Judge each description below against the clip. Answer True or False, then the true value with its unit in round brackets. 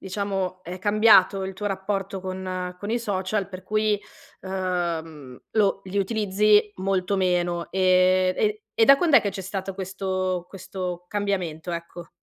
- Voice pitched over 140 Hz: True (190 Hz)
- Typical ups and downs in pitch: False (1.7 semitones)